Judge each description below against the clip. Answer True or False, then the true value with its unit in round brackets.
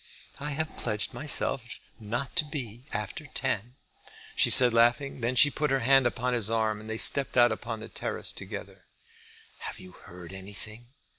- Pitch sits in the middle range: False (120 Hz)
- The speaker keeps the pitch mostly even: False (3.7 semitones)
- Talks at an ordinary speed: True (170 wpm)